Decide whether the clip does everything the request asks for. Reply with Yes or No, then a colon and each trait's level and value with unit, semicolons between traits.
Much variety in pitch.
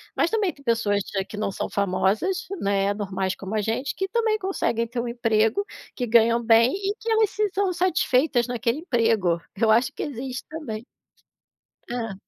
Yes: wide, 8.4 semitones